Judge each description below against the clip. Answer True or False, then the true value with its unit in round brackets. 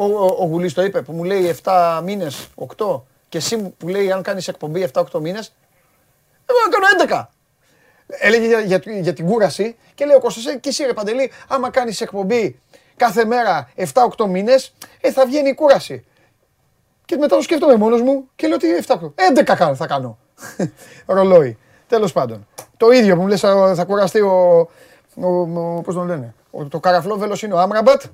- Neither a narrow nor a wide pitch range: False (6.2 semitones)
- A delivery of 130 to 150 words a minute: False (170 wpm)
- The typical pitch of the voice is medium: False (200 Hz)